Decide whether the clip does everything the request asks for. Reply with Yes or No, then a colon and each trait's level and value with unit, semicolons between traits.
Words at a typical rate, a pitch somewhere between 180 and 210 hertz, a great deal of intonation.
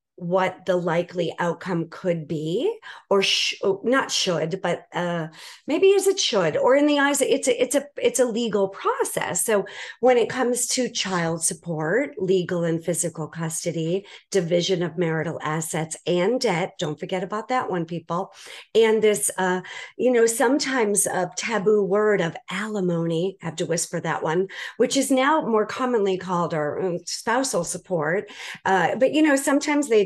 Yes: average, 170 wpm; high, 190 Hz; wide, 6.2 semitones